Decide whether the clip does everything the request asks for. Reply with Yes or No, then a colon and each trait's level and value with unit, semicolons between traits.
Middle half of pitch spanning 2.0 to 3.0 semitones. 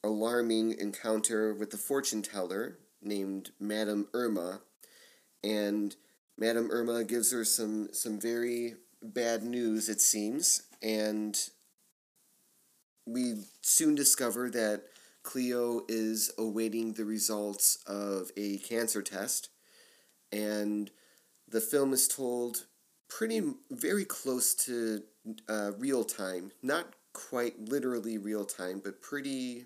Yes: narrow, 2.4 semitones